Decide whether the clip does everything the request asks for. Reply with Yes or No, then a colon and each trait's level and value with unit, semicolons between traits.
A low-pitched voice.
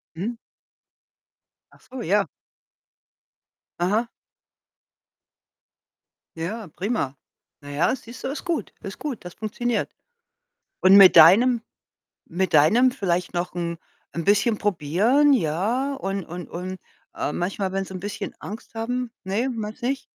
No: high, 200 Hz